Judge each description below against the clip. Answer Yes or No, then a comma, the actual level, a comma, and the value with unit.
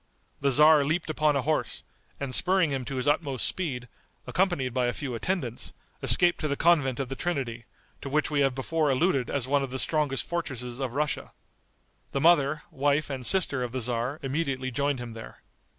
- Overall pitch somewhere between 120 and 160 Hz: Yes, medium, 140 Hz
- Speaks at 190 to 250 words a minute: Yes, average, 195 wpm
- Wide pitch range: No, average, 3.1 semitones